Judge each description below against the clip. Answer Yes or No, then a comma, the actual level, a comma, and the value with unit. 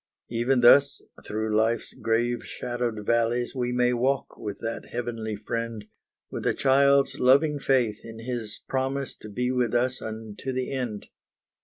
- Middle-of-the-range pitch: No, low, 120 Hz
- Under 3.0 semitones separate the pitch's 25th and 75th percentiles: Yes, narrow, 2.4 semitones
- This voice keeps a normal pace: Yes, average, 150 wpm